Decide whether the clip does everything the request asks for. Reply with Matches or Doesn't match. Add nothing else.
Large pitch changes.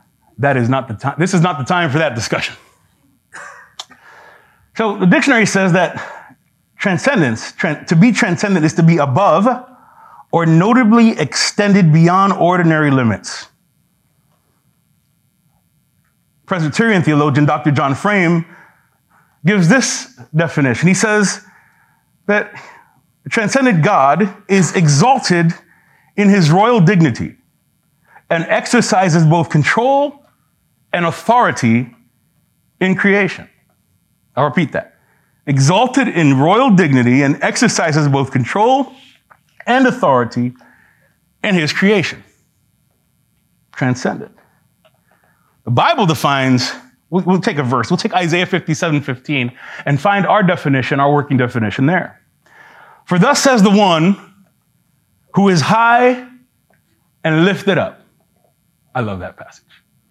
Matches